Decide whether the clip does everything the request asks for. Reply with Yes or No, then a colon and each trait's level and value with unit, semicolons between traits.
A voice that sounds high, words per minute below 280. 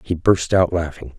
No: very low, 85 Hz; fast, 205 wpm